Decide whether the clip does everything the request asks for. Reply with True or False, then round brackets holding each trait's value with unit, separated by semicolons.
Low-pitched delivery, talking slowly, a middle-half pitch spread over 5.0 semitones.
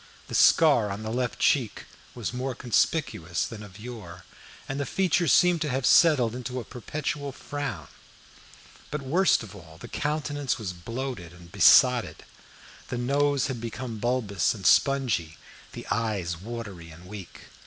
False (120 Hz; 155 wpm; 5.5 semitones)